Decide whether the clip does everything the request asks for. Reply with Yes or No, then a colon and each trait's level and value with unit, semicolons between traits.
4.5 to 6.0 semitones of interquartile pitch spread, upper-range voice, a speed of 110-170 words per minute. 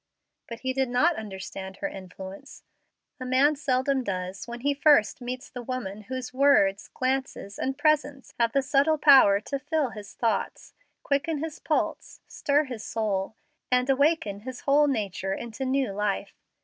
Yes: average, 5.2 semitones; very high, 255 Hz; average, 160 wpm